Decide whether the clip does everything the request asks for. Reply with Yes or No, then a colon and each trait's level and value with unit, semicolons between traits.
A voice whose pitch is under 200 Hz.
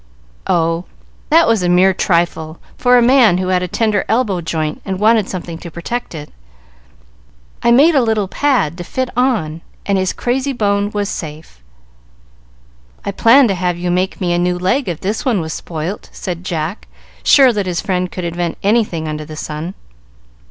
Yes: medium, 185 Hz